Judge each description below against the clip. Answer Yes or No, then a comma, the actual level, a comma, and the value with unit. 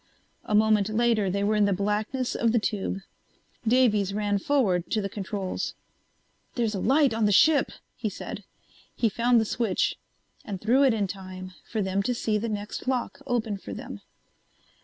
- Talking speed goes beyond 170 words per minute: Yes, average, 180 wpm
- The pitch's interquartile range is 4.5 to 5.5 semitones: No, average, 2.8 semitones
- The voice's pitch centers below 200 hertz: No, high, 215 Hz